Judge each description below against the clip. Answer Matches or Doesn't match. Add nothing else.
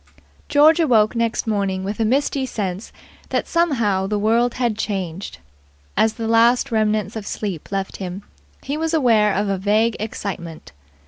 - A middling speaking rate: Matches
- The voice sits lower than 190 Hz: Doesn't match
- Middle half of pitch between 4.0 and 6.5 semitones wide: Doesn't match